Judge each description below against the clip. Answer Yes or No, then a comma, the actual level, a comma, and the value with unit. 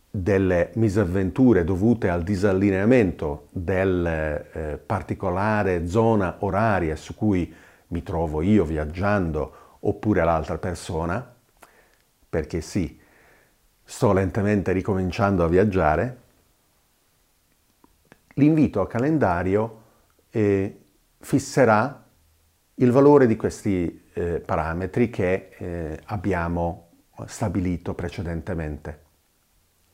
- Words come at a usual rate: No, slow, 85 wpm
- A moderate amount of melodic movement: Yes, average, 3.9 semitones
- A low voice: Yes, very low, 95 Hz